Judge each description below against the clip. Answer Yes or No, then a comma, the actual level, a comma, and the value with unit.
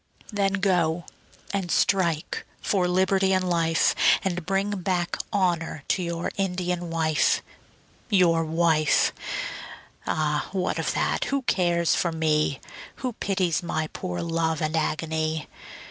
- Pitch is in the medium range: Yes, medium, 170 Hz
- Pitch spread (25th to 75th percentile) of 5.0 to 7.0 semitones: No, average, 2.8 semitones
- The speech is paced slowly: Yes, slow, 125 wpm